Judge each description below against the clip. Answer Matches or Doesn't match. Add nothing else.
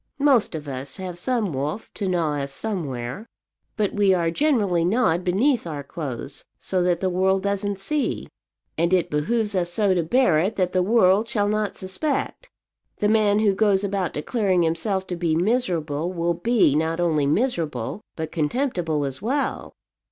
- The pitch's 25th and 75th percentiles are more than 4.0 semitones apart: Matches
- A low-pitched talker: Doesn't match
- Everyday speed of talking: Matches